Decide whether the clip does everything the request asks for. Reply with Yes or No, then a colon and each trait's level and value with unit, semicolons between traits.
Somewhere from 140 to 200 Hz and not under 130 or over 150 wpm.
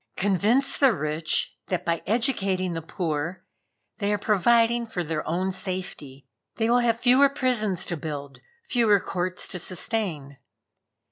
Yes: high, 190 Hz; average, 140 wpm